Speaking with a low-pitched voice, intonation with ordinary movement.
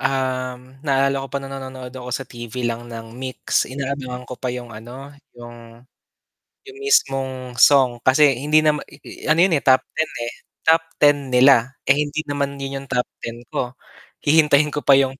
No: low, 130 Hz; narrow, 2.1 semitones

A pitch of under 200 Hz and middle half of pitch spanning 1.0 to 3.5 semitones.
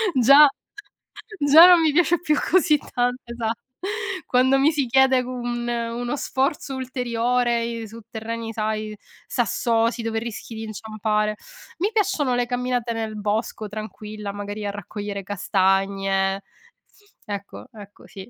No: high, 230 Hz; average, 3.1 semitones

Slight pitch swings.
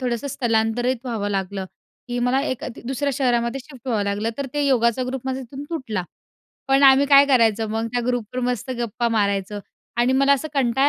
No: average, 3.0 semitones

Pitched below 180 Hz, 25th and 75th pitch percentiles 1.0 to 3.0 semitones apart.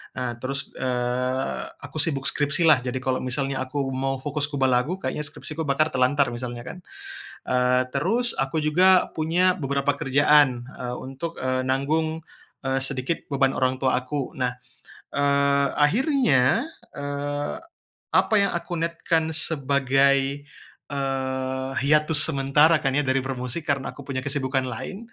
Yes: medium, 140 Hz; narrow, 2.6 semitones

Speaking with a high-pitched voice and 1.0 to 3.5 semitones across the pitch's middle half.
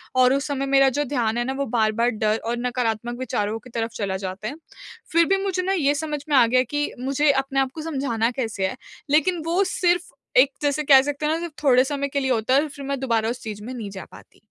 No: very high, 265 Hz; average, 4.0 semitones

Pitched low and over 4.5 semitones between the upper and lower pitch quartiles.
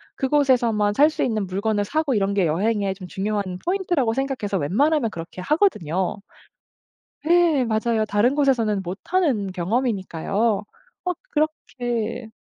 No: high, 220 Hz; wide, 5.6 semitones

